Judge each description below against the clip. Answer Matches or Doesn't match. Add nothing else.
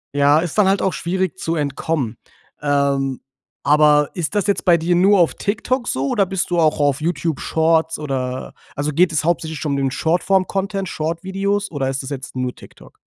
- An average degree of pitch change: Matches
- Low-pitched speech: Doesn't match